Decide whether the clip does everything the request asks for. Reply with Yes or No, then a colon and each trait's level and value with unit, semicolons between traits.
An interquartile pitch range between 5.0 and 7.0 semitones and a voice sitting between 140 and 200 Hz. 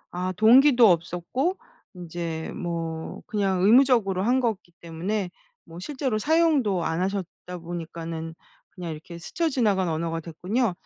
Yes: wide, 5.6 semitones; medium, 185 Hz